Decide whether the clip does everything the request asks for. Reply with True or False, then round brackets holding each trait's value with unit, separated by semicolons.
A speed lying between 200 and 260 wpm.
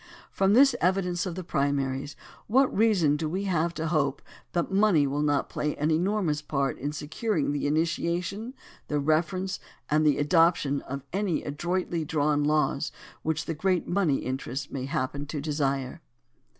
False (155 wpm)